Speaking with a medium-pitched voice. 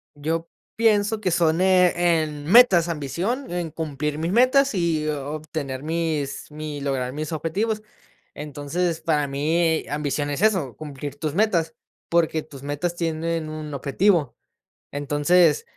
Yes: medium, 160 Hz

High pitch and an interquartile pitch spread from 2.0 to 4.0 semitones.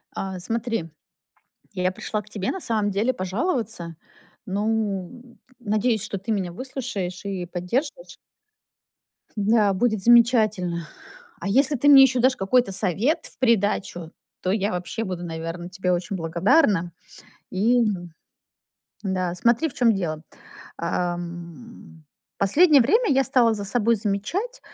No: high, 205 Hz; average, 4.9 semitones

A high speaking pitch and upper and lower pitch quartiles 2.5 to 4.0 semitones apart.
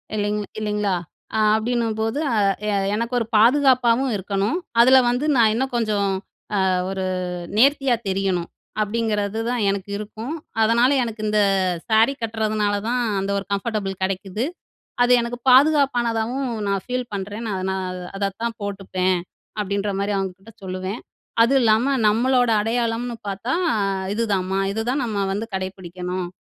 Yes: high, 220 Hz; average, 3.3 semitones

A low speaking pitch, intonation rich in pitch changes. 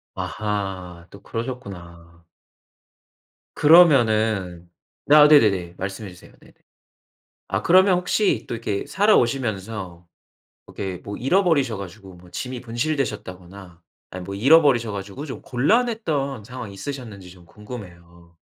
Yes: low, 105 Hz; wide, 6.7 semitones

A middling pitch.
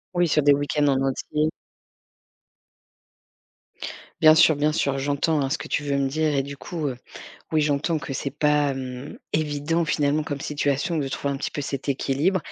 Yes: medium, 145 Hz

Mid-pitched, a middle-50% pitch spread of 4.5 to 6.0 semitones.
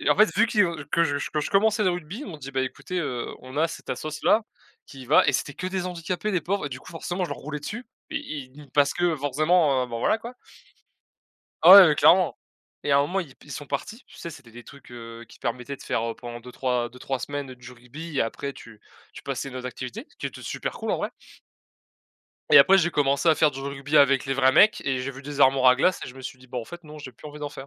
Yes: medium, 145 Hz; average, 5.0 semitones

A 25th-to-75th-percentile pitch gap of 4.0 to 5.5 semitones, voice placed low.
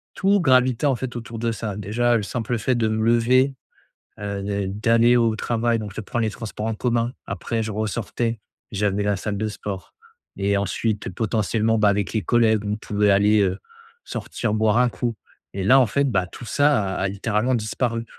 No: narrow, 2.5 semitones; low, 110 Hz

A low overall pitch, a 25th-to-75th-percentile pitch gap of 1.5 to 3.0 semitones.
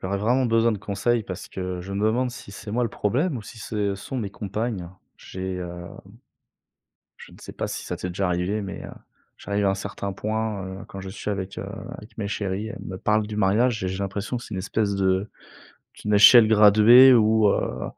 Yes: low, 105 Hz; narrow, 2.4 semitones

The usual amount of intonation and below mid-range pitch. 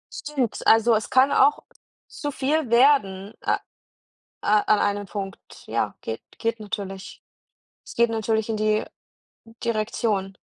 No: average, 3.0 semitones; high, 220 Hz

